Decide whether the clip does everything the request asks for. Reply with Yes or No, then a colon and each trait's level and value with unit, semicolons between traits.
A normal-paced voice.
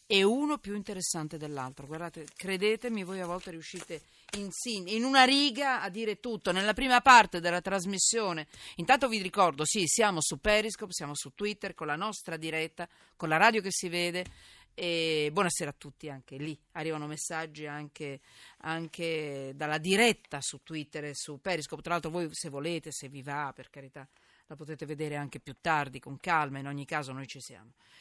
No: fast, 180 wpm